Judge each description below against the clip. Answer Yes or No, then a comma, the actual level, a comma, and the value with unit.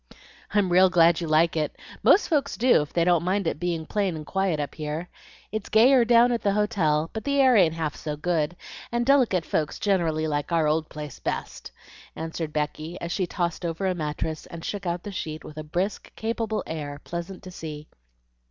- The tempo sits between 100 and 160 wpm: No, fast, 205 wpm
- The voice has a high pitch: No, medium, 170 Hz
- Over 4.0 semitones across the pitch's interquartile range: Yes, average, 4.5 semitones